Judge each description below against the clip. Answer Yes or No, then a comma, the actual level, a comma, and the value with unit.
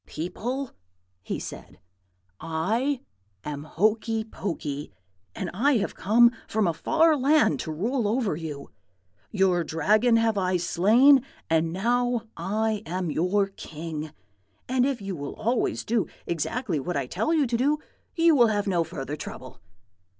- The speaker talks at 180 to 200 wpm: No, average, 145 wpm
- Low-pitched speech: No, high, 205 Hz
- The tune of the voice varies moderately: No, wide, 6.5 semitones